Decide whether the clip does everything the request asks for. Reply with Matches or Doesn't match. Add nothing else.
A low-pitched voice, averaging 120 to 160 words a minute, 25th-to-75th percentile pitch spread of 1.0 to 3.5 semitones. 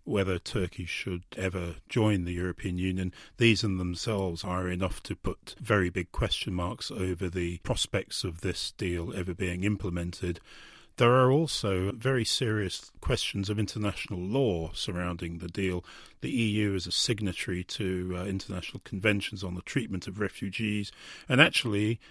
Matches